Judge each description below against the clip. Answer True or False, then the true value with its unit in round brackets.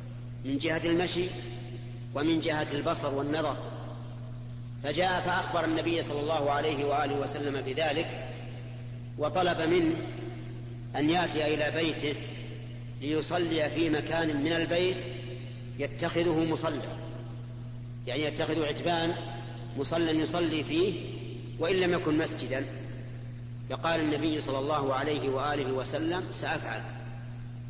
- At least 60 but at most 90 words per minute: False (100 wpm)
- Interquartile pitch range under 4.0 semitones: False (4.9 semitones)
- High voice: False (140 Hz)